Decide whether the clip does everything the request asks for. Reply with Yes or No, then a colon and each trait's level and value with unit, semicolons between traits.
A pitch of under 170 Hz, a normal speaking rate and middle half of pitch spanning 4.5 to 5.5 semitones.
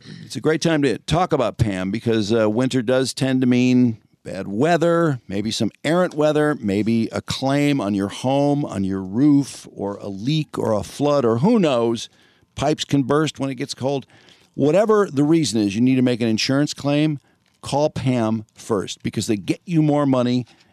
Yes: low, 135 Hz; average, 190 wpm; average, 4.8 semitones